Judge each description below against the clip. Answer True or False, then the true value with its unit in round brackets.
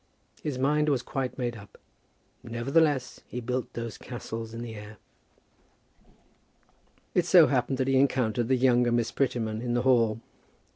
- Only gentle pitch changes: True (2.3 semitones)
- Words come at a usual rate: True (150 wpm)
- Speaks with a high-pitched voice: False (120 Hz)